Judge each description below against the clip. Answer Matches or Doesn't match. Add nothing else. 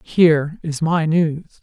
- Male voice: Doesn't match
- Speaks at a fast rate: Doesn't match